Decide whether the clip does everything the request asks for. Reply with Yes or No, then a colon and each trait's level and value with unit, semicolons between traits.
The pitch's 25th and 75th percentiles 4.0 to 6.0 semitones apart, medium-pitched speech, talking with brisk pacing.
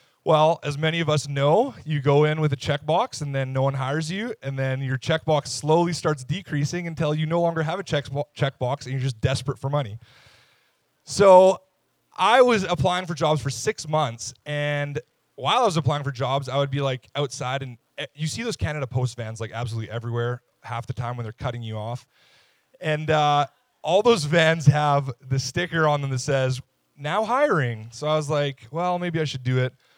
No: average, 3.1 semitones; medium, 145 Hz; fast, 210 wpm